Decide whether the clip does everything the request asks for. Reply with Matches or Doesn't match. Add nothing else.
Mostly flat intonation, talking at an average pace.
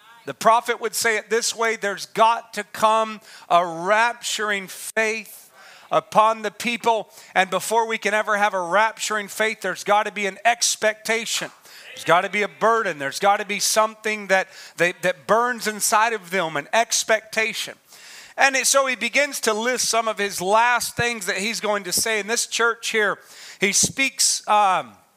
Matches